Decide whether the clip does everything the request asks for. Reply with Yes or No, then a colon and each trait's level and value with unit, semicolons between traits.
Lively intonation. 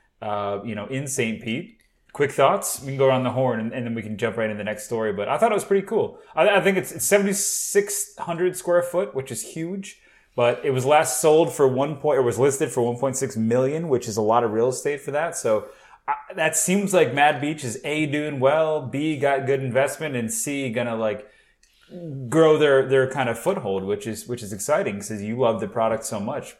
Yes: wide, 5.7 semitones